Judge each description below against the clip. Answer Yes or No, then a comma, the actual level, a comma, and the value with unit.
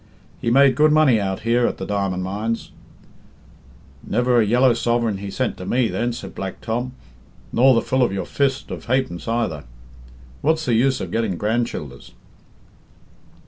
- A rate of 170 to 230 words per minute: Yes, average, 175 wpm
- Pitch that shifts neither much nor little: Yes, average, 3.7 semitones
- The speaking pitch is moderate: No, low, 120 Hz